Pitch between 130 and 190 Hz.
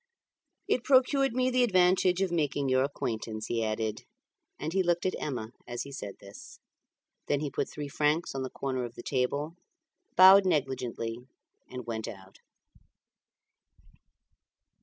Yes: medium, 140 Hz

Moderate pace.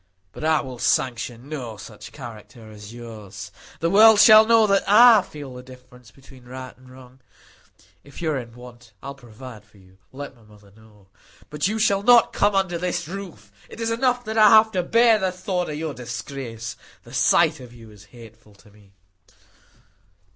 Yes: average, 190 wpm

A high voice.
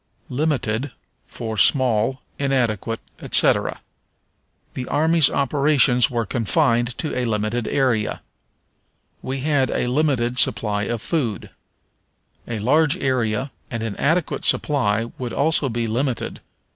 No: low, 125 Hz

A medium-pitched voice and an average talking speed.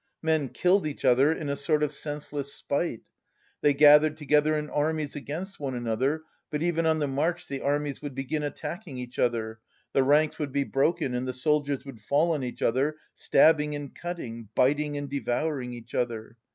Yes: medium, 145 Hz; average, 185 wpm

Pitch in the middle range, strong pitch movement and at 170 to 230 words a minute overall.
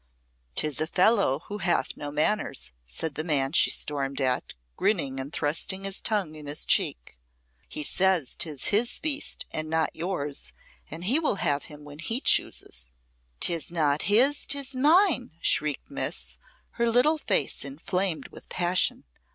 No: medium, 160 Hz; wide, 6.2 semitones; average, 155 wpm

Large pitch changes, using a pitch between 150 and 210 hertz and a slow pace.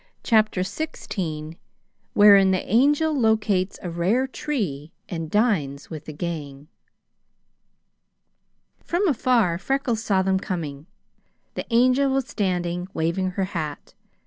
Yes: wide, 6.2 semitones; high, 190 Hz; slow, 115 wpm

